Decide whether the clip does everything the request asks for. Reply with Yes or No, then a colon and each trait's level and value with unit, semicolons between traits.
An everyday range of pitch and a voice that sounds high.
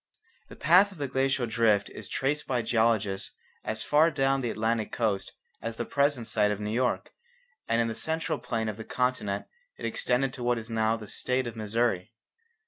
No: average, 3.2 semitones; low, 115 Hz